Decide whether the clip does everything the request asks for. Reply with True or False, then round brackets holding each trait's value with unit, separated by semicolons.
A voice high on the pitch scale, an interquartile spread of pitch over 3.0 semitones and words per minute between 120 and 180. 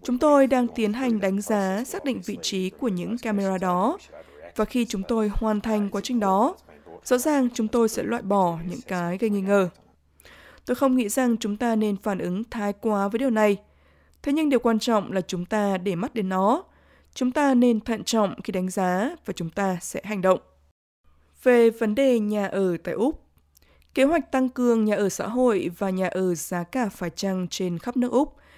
False (210 Hz; 4.4 semitones; 215 wpm)